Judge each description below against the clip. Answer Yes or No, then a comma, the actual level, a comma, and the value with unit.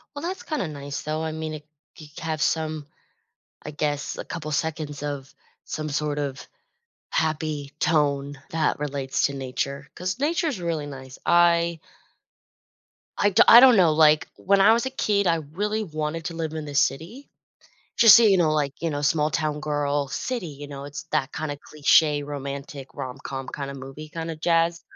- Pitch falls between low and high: Yes, medium, 155 Hz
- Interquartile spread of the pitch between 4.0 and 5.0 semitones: No, average, 2.7 semitones